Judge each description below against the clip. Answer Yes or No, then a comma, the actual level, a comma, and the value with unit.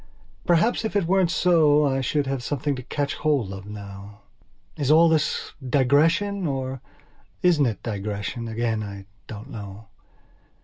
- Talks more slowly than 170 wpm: Yes, average, 145 wpm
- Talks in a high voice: No, low, 135 Hz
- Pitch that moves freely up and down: Yes, wide, 6.4 semitones